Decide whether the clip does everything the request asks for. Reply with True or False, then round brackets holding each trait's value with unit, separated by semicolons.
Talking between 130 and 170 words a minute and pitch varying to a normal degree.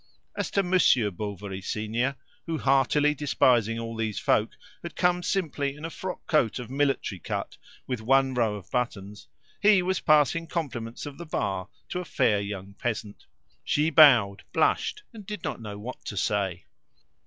False (165 wpm; 6.7 semitones)